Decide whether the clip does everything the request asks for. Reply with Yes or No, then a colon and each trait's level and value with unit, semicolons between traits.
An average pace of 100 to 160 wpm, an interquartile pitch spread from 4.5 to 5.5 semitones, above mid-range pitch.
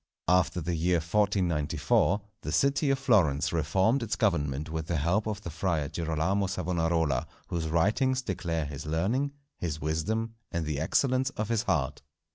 No: average, 155 wpm; average, 5.2 semitones; very low, 85 Hz